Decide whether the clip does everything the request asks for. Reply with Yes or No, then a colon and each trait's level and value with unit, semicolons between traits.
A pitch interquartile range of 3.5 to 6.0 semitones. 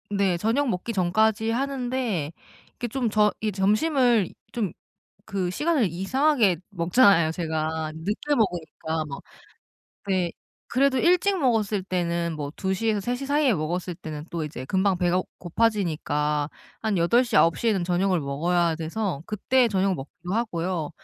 Yes: average, 5.3 semitones